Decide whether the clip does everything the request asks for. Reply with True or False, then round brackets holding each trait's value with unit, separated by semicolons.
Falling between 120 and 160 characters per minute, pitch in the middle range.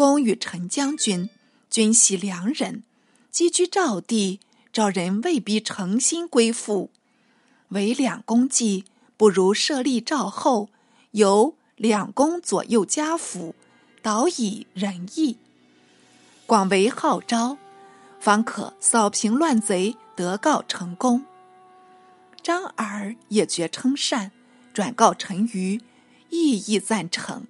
False (155 characters per minute; 225 Hz)